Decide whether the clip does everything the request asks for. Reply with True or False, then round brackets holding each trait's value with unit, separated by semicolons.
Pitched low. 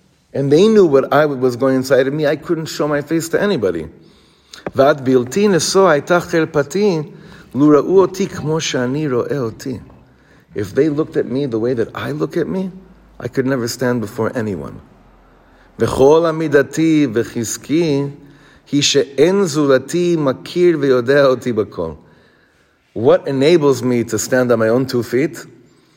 False (145 Hz)